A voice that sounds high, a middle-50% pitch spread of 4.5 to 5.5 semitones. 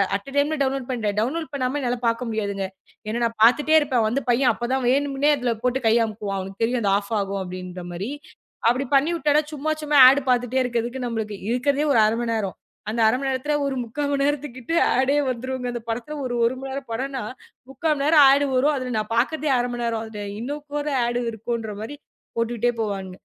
No: high, 245 Hz; average, 3.6 semitones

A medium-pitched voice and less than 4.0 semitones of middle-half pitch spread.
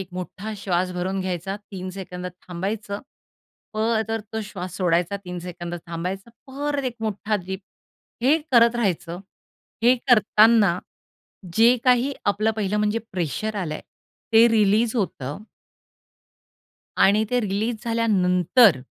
No: high, 205 Hz; average, 3.6 semitones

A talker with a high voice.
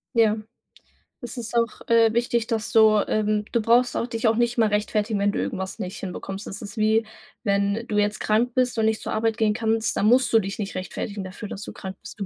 Yes: high, 220 Hz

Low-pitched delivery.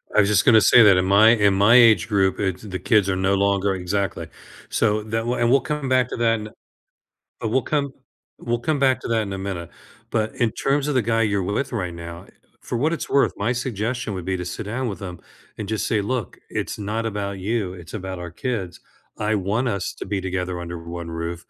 Yes: low, 105 Hz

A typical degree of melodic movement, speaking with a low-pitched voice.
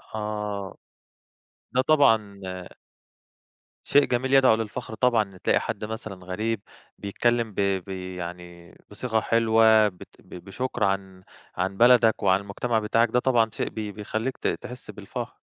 Yes: average, 3.3 semitones; low, 110 Hz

